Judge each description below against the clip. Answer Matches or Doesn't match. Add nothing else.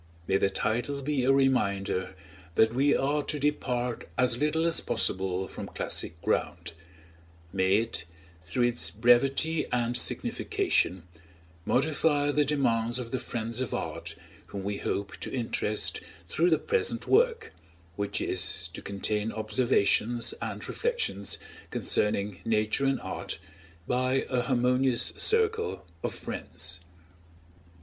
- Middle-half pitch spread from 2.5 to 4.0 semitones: Doesn't match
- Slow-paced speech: Matches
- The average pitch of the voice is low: Matches